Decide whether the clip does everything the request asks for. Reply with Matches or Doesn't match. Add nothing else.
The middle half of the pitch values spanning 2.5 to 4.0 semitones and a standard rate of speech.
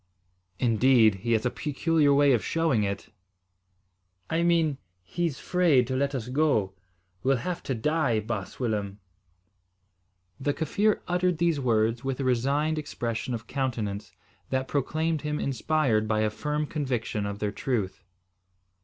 Doesn't match